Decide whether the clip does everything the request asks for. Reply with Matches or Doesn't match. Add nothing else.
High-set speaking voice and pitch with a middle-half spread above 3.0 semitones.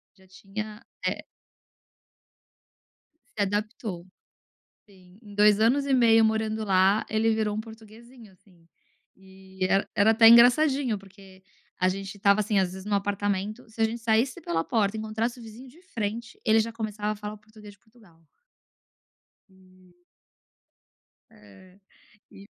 Doesn't match